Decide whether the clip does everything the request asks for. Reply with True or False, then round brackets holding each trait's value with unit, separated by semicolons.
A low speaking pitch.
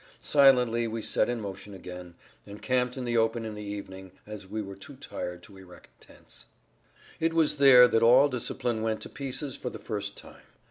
True (115 Hz)